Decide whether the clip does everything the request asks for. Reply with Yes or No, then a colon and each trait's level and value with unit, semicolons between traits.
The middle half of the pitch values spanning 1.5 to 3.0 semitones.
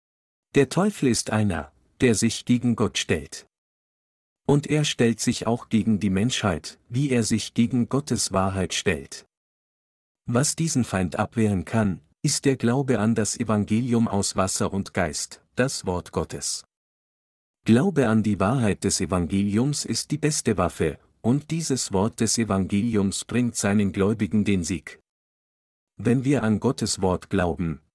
No: average, 3.9 semitones